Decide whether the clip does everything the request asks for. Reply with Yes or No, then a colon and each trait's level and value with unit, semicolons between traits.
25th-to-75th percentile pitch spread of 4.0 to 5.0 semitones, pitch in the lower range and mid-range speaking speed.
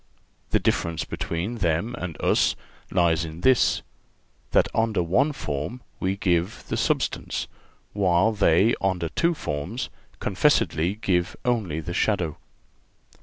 No: average, 4.7 semitones; very low, 90 Hz; slow, 120 wpm